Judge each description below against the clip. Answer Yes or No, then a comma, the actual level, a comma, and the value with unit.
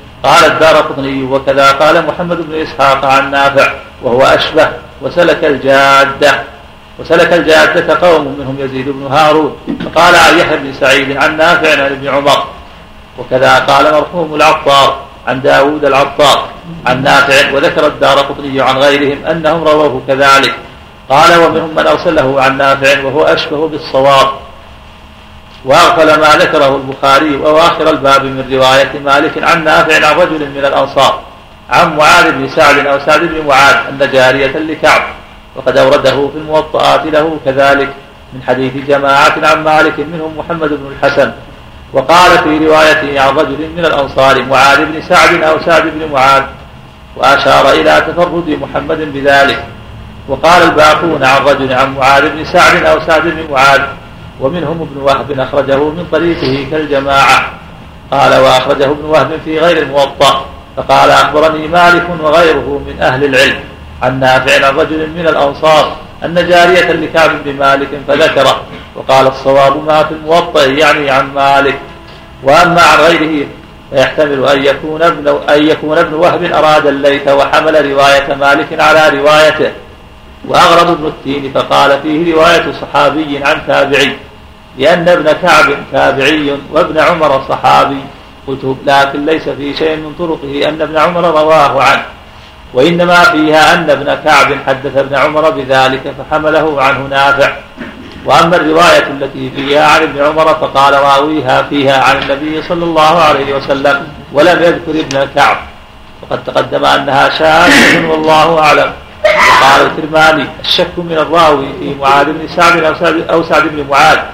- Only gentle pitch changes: Yes, narrow, 2.3 semitones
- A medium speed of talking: No, fast, 140 wpm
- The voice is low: No, medium, 145 Hz